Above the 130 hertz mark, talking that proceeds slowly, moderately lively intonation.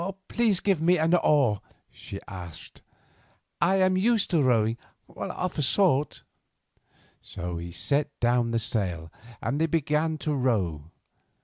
No: medium, 140 Hz; slow, 130 wpm; wide, 7.9 semitones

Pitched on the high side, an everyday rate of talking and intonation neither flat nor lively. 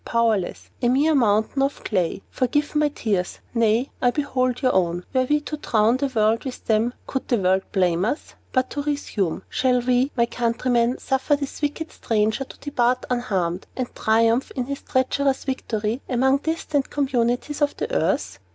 Yes: very high, 250 Hz; average, 170 wpm; average, 3.9 semitones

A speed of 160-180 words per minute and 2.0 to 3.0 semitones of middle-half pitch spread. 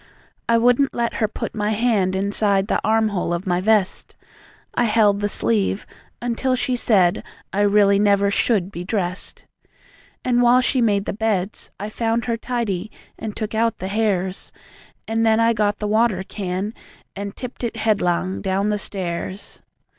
Yes: average, 170 wpm; average, 2.7 semitones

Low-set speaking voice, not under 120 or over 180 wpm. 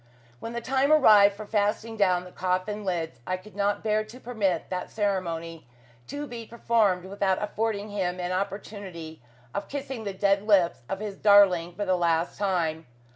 No: high, 200 Hz; average, 175 wpm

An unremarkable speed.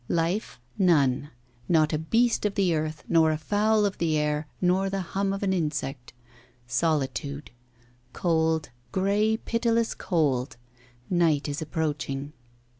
No: slow, 130 wpm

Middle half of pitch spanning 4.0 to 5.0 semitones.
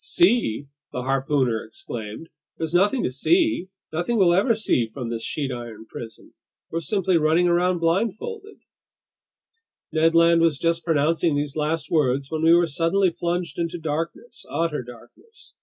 Yes: average, 4.3 semitones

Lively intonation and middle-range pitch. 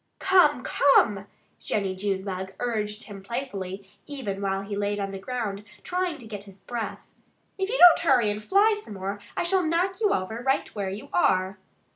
No: wide, 6.4 semitones; high, 210 Hz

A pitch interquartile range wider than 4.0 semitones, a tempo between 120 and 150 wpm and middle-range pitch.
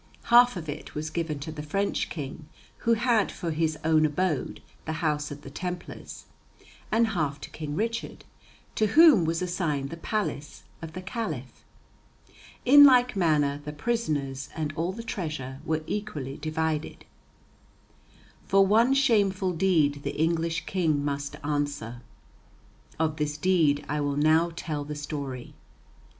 Yes: average, 4.6 semitones; average, 145 wpm; medium, 160 Hz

